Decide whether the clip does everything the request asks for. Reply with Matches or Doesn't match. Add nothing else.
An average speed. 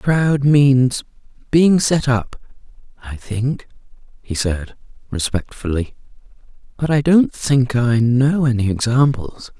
Doesn't match